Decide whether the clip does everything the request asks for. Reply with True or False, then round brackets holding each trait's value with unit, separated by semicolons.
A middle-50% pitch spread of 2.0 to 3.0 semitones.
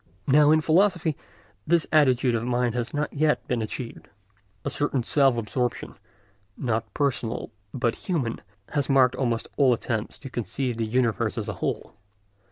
False (3.8 semitones)